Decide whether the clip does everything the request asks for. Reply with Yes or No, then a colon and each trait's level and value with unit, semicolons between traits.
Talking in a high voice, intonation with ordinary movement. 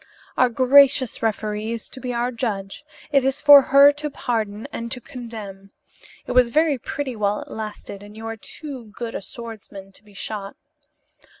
Yes: high, 230 Hz; average, 3.7 semitones